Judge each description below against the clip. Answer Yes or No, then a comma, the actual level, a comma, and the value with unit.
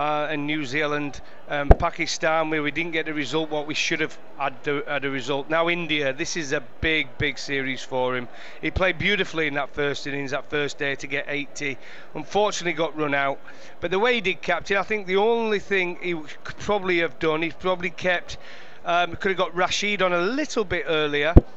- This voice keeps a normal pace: No, fast, 215 wpm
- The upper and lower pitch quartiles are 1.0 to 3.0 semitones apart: No, average, 3.6 semitones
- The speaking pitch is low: No, medium, 160 Hz